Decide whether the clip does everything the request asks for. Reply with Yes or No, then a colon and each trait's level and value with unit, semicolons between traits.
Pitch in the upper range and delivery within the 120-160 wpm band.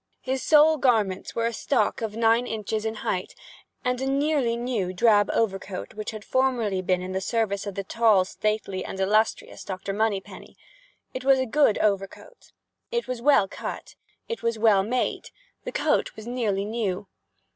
No: high, 220 Hz; average, 170 wpm